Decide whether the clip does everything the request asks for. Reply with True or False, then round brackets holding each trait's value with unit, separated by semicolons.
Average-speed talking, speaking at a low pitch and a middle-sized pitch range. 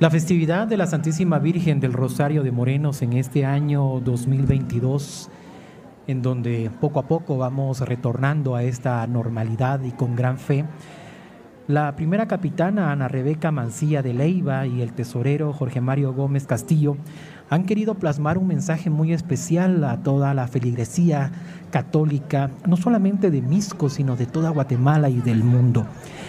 False (150 wpm; 145 Hz; 3.9 semitones)